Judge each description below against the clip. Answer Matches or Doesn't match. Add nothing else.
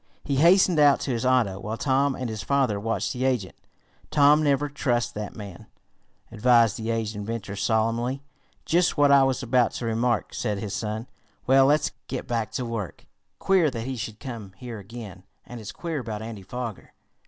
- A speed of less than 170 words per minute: Doesn't match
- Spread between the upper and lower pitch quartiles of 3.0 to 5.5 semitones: Matches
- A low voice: Matches